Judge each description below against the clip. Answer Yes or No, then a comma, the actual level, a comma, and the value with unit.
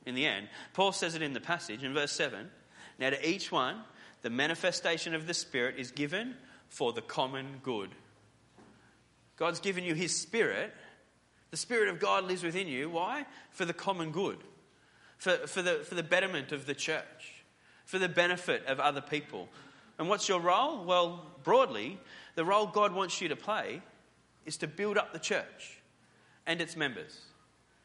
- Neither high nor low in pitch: Yes, medium, 170 Hz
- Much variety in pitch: No, average, 4.2 semitones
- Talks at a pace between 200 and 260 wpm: No, average, 175 wpm